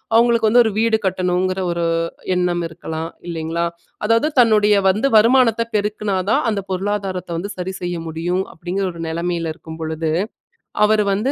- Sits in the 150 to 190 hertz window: Yes, medium, 185 Hz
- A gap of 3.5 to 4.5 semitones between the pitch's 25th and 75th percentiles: Yes, average, 3.9 semitones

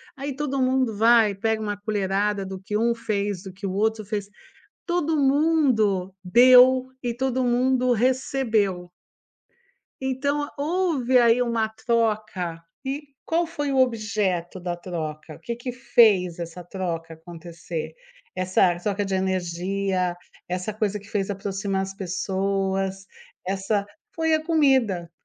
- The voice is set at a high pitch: Yes, high, 210 Hz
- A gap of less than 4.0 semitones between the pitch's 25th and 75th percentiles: No, average, 5.0 semitones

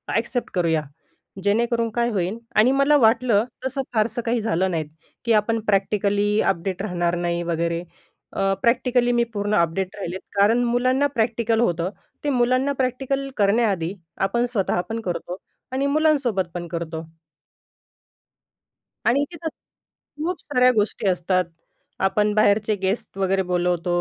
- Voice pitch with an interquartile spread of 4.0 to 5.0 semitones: Yes, average, 4.6 semitones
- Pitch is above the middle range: Yes, high, 215 Hz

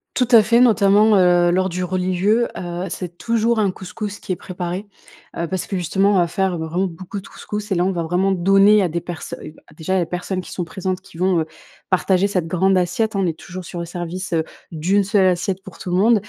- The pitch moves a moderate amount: No, narrow, 2.1 semitones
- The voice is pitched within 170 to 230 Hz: Yes, medium, 185 Hz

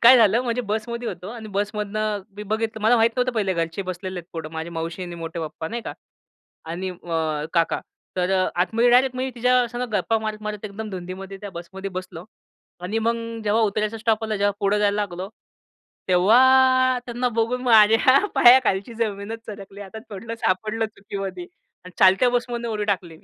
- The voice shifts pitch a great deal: No, average, 3.7 semitones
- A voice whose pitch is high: Yes, high, 210 Hz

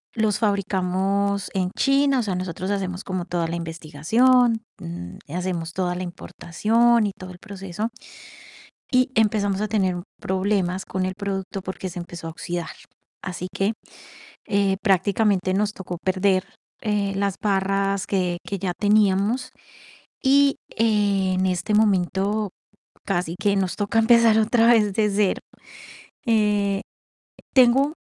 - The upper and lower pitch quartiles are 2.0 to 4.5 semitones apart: Yes, narrow, 2.6 semitones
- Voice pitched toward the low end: No, high, 195 Hz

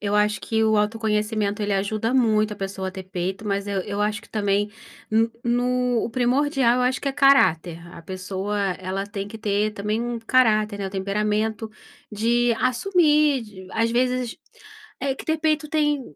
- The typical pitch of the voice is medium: No, high, 215 Hz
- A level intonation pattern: No, average, 3.6 semitones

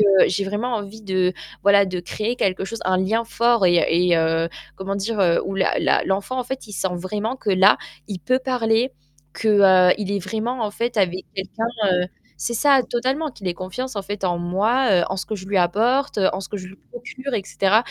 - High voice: Yes, high, 200 Hz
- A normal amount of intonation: Yes, average, 3.7 semitones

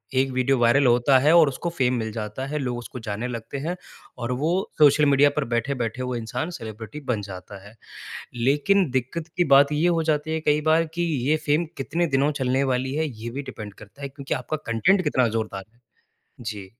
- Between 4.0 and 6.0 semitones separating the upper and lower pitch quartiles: Yes, average, 4.3 semitones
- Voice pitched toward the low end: Yes, low, 130 Hz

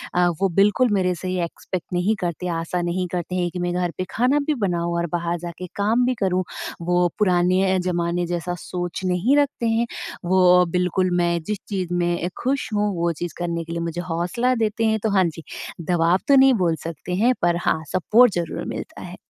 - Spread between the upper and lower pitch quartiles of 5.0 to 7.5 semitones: No, average, 2.9 semitones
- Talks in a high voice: No, medium, 180 Hz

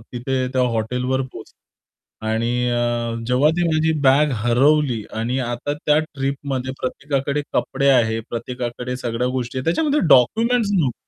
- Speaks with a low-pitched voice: Yes, low, 130 Hz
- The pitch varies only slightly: No, average, 3.5 semitones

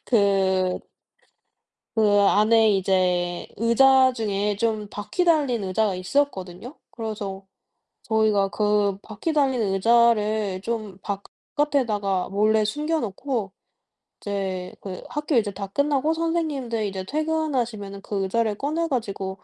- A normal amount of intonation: Yes, average, 4.8 semitones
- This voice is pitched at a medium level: No, high, 215 Hz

